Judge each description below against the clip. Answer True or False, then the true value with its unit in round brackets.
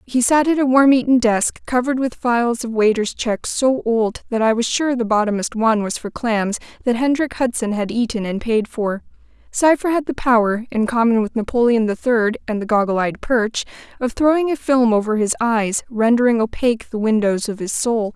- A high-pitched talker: True (235 Hz)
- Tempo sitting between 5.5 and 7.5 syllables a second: False (5.3 syllables/s)